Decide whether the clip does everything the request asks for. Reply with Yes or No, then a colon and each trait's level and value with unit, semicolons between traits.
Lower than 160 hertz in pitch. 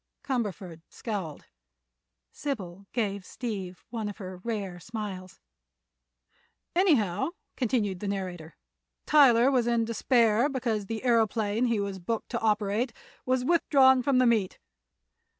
No: high, 220 Hz